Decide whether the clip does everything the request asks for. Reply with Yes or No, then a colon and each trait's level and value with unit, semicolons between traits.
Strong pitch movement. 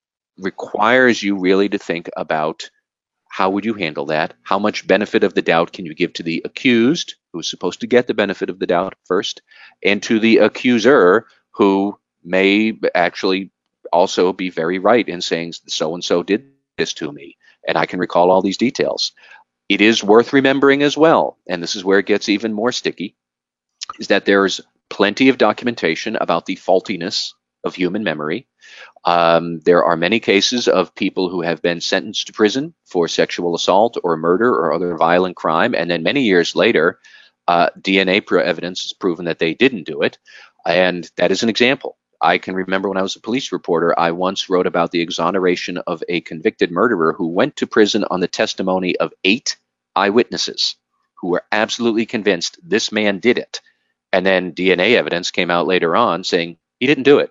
No: average, 4.2 semitones